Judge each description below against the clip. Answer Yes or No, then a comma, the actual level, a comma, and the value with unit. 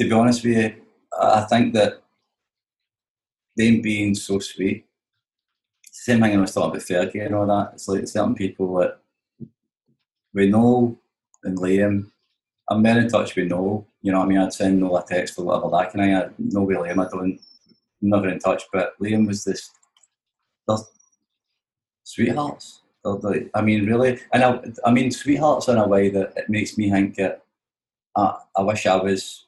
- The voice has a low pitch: Yes, low, 100 Hz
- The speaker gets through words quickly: No, average, 185 wpm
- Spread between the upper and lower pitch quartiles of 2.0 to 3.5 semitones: Yes, narrow, 2.6 semitones